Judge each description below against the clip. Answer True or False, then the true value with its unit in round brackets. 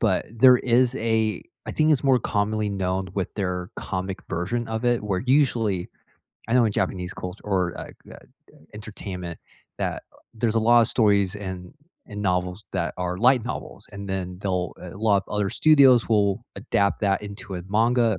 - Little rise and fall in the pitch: False (3.7 semitones)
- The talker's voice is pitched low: True (105 Hz)